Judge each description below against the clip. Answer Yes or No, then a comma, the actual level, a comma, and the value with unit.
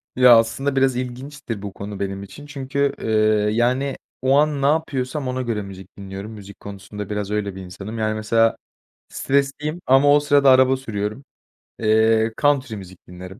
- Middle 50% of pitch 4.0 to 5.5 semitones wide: Yes, average, 5.1 semitones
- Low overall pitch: Yes, low, 115 Hz